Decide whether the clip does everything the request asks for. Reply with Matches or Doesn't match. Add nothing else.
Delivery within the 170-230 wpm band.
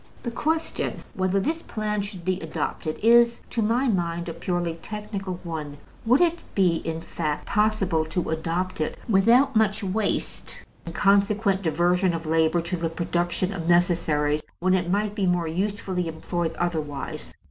Doesn't match